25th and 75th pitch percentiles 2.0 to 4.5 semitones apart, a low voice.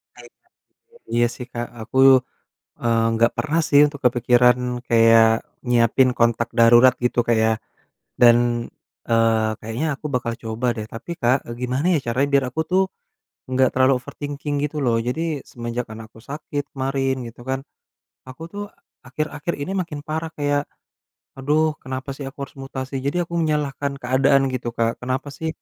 Yes: average, 3.4 semitones; low, 130 Hz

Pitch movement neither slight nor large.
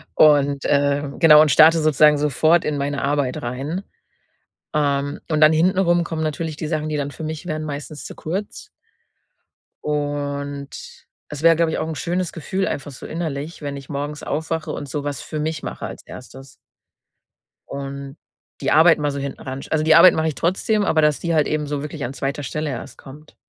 No: narrow, 2.0 semitones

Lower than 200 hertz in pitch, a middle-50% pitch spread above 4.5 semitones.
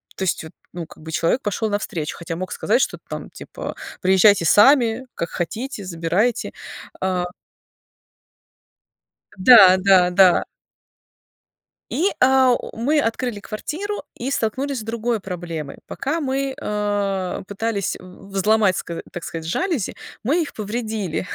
No: high, 205 Hz; average, 5.1 semitones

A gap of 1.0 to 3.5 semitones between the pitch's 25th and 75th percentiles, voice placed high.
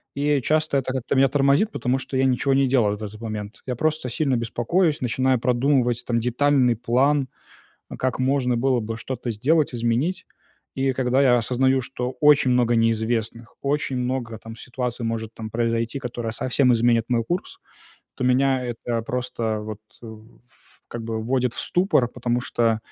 No: narrow, 2.6 semitones; low, 125 Hz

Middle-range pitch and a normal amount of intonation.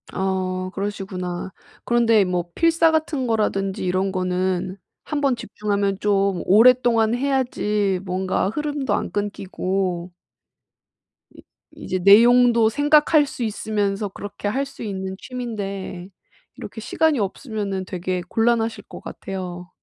No: high, 205 Hz; average, 4.1 semitones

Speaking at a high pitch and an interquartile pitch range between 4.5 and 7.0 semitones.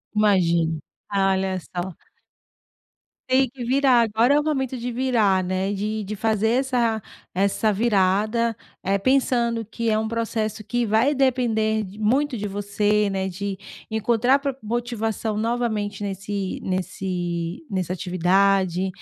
No: high, 215 Hz; average, 3.6 semitones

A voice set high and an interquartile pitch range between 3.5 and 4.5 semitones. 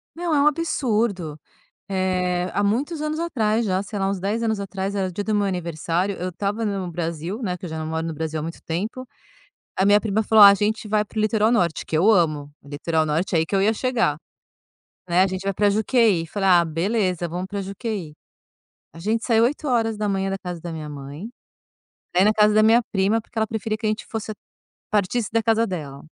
Yes: high, 200 Hz; average, 4.0 semitones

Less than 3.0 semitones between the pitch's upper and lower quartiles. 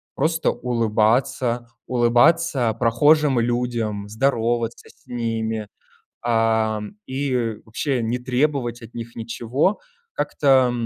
Yes: narrow, 2.5 semitones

